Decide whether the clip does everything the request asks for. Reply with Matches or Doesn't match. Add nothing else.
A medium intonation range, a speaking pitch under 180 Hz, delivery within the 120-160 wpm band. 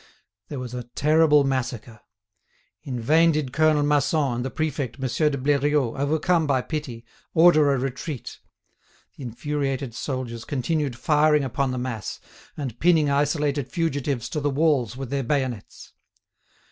Matches